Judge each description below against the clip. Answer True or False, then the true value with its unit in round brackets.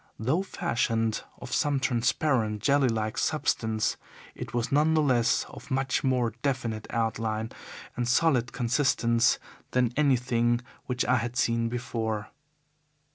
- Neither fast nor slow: False (130 wpm)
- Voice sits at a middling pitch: False (120 Hz)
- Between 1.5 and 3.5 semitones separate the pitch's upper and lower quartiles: True (2.6 semitones)